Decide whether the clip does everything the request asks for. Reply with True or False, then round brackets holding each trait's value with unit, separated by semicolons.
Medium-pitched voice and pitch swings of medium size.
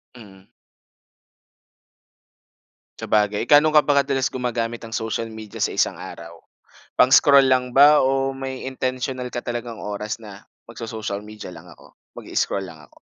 False (120 Hz; 3.8 semitones)